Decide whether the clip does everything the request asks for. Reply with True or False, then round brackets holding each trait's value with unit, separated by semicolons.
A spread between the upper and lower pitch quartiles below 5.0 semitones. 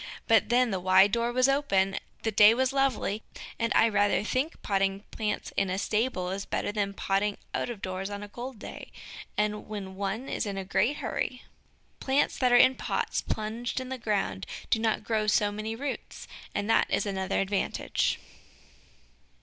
True (3.5 semitones)